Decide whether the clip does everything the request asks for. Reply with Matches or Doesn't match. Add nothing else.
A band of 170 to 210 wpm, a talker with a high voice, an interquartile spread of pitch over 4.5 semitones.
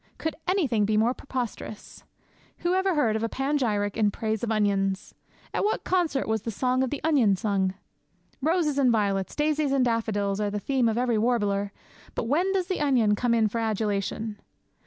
Matches